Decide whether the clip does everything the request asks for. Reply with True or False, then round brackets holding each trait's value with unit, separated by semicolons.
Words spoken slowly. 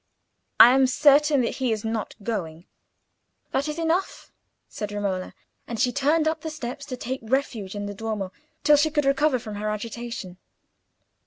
False (170 wpm)